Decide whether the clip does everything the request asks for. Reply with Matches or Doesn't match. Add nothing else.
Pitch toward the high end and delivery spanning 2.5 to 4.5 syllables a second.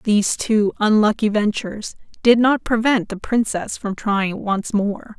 Matches